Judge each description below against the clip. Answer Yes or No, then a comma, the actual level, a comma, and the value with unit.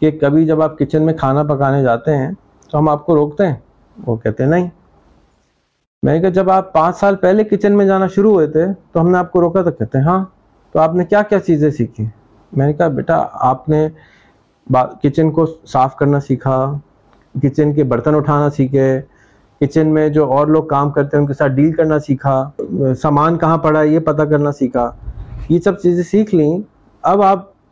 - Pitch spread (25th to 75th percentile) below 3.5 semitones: No, average, 3.9 semitones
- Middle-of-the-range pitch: Yes, medium, 150 Hz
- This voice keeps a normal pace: No, fast, 205 wpm